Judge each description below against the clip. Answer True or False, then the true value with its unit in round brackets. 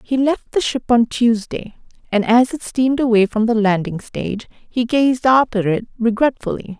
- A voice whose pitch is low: False (235 Hz)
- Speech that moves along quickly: False (175 wpm)